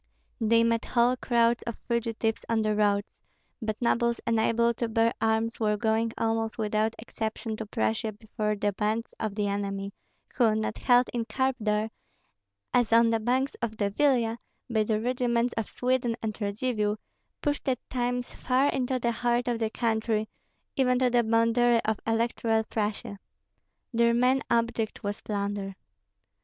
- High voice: Yes, high, 230 Hz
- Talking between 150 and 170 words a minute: Yes, average, 160 wpm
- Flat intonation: Yes, narrow, 1.8 semitones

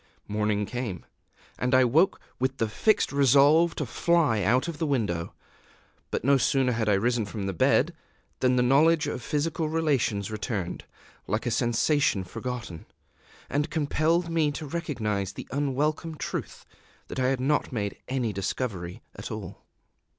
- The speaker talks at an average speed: Yes, average, 150 wpm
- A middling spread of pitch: No, wide, 5.8 semitones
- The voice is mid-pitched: No, low, 130 Hz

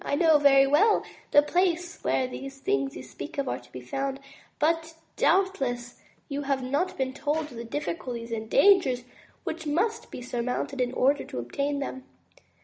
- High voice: Yes, very high, 275 Hz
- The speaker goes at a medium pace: Yes, average, 180 wpm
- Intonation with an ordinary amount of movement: Yes, average, 4.3 semitones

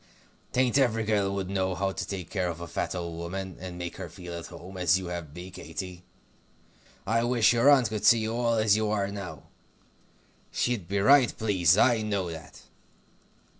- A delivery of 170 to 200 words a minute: Yes, average, 195 wpm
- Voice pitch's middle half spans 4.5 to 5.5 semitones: No, average, 3.8 semitones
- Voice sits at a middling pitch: No, low, 100 Hz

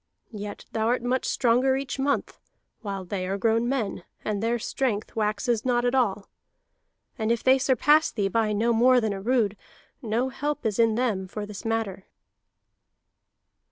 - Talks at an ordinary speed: Yes, average, 165 wpm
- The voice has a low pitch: No, high, 230 Hz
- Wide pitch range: No, average, 3.4 semitones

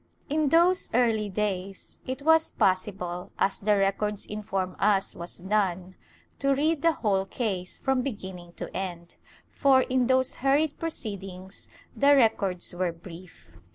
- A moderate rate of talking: Yes, average, 145 wpm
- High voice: Yes, high, 205 Hz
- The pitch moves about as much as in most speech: No, wide, 6.0 semitones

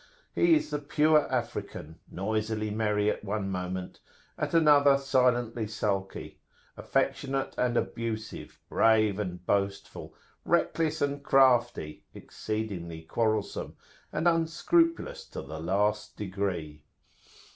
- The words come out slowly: Yes, slow, 105 wpm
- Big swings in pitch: Yes, wide, 5.9 semitones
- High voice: No, low, 110 Hz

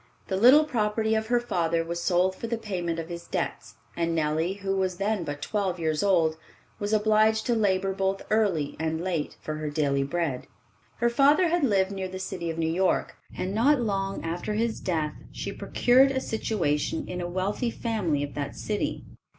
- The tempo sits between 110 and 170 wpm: No, average, 190 wpm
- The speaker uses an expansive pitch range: No, average, 4.7 semitones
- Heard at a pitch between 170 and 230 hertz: Yes, high, 190 Hz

